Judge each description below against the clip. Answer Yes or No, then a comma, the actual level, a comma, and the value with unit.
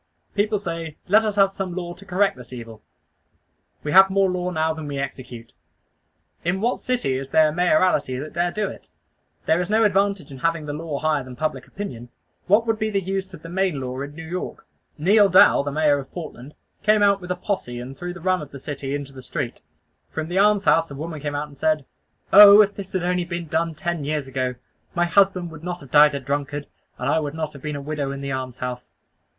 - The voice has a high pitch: No, medium, 160 Hz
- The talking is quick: Yes, fast, 235 wpm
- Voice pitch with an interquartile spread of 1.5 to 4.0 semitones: No, average, 5.0 semitones